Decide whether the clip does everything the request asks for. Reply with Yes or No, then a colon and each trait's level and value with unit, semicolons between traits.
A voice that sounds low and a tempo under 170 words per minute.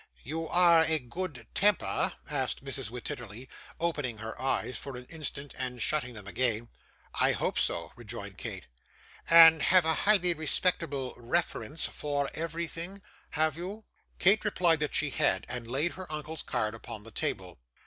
No: medium, 145 Hz; average, 155 wpm